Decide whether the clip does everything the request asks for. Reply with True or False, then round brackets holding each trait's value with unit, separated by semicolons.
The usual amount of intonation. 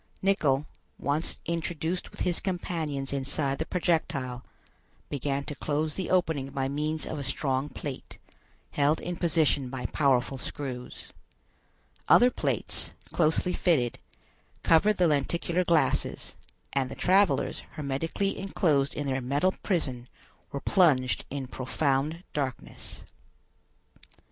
True (3.8 semitones)